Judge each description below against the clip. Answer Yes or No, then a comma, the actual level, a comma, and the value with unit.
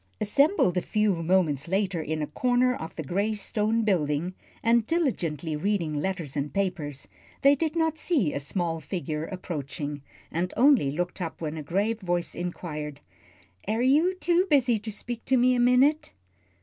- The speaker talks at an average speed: Yes, average, 165 wpm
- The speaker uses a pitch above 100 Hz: Yes, high, 190 Hz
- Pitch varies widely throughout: Yes, wide, 7.5 semitones